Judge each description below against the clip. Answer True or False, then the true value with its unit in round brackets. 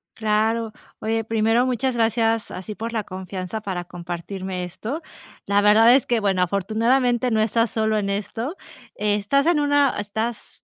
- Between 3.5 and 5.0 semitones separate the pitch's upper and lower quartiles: False (2.7 semitones)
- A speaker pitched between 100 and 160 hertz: False (220 Hz)